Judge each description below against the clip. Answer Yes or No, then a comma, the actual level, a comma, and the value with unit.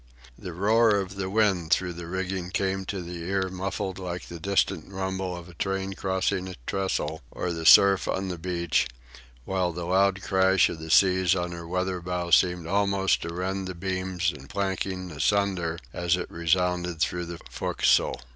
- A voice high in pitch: No, very low, 90 Hz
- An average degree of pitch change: No, narrow, 1.7 semitones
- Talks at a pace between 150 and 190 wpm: Yes, average, 180 wpm